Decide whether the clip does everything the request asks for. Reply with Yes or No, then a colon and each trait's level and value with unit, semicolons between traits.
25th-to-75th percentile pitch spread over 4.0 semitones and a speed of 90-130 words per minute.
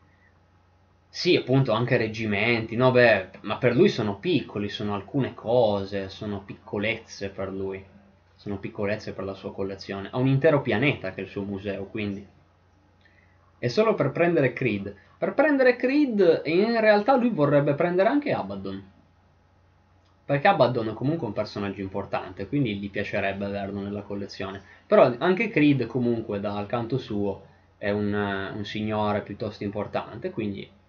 No: average, 4.4 semitones; average, 150 wpm